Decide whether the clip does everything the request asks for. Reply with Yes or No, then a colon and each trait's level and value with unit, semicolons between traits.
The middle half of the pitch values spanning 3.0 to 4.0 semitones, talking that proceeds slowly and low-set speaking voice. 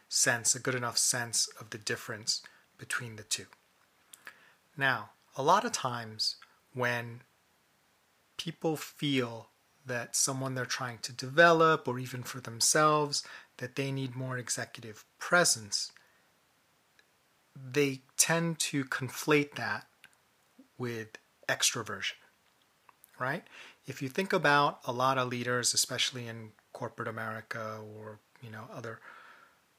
Yes: average, 3.5 semitones; slow, 120 wpm; low, 130 Hz